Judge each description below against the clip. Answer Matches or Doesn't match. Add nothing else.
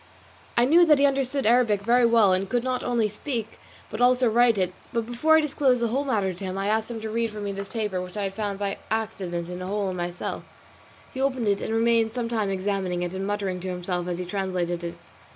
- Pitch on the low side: Doesn't match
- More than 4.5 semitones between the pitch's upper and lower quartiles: Doesn't match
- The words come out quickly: Matches